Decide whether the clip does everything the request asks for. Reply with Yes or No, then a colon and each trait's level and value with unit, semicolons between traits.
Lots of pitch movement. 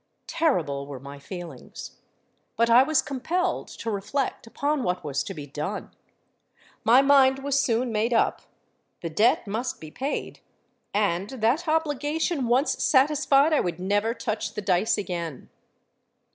Yes: wide, 7.4 semitones